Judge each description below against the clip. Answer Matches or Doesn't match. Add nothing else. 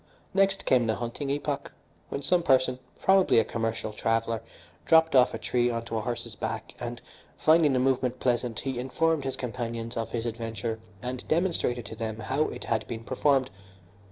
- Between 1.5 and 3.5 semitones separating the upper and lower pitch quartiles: Matches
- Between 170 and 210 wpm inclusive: Matches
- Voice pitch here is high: Doesn't match